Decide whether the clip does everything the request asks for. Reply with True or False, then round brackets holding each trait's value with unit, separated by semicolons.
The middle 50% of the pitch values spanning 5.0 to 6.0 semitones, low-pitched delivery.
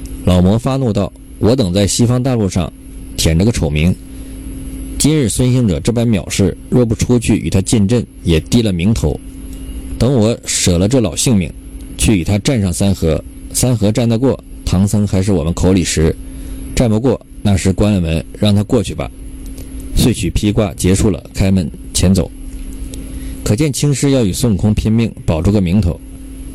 True (5.5 semitones; 100 Hz)